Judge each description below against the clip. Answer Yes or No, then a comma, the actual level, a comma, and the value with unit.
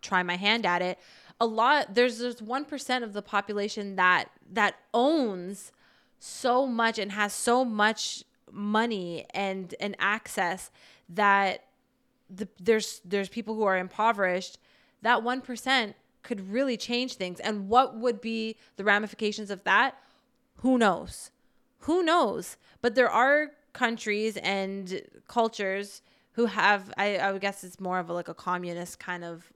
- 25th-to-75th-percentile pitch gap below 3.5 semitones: No, average, 3.8 semitones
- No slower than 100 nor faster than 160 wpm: Yes, average, 150 wpm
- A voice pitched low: No, high, 210 Hz